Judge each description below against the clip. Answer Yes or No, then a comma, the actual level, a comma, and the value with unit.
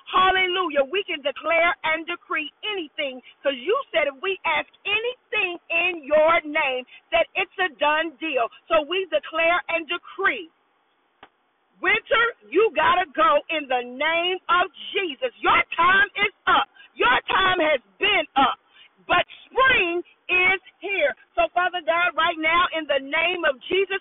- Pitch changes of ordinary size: Yes, average, 3.6 semitones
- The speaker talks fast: No, average, 150 wpm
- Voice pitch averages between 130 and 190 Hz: No, very high, 345 Hz